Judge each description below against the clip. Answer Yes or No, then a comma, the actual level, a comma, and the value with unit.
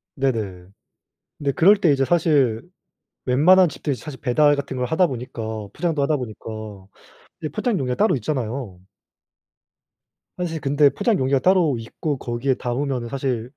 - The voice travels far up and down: No, average, 4.0 semitones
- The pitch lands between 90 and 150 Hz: Yes, medium, 140 Hz